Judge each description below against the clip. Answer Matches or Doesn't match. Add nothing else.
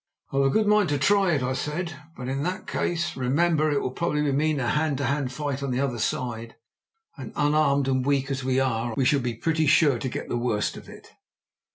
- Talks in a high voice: Doesn't match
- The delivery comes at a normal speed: Doesn't match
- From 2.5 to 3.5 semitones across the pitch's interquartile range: Matches